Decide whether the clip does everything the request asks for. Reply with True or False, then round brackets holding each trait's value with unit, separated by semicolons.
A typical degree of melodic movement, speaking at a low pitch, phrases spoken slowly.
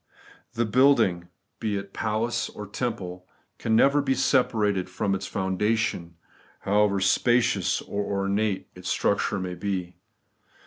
True (3.2 semitones; 105 Hz; 125 wpm)